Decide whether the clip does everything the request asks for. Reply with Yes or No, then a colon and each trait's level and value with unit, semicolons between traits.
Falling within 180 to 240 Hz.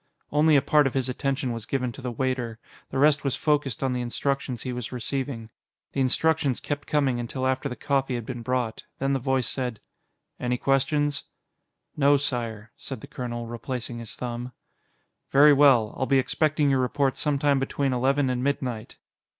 No: low, 130 Hz